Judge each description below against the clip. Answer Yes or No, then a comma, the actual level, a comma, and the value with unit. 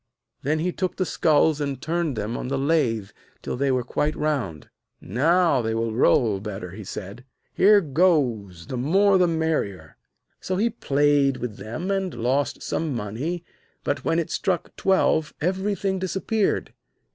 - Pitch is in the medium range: Yes, medium, 145 Hz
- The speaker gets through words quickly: No, average, 155 wpm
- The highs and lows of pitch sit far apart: Yes, wide, 7.1 semitones